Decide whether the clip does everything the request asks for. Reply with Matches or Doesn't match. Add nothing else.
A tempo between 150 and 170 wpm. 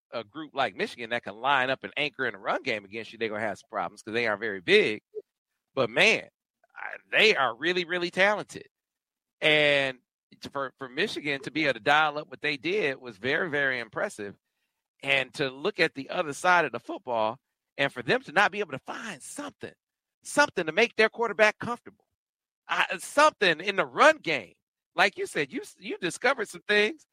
Doesn't match